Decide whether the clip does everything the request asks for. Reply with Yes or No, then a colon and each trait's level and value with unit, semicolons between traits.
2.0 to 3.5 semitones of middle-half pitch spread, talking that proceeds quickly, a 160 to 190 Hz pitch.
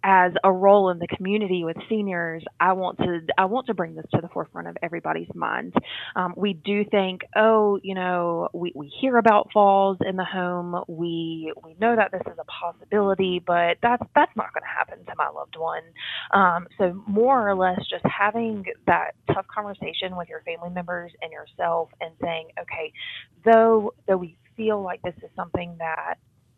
No: average, 3.1 semitones; average, 190 wpm; medium, 185 Hz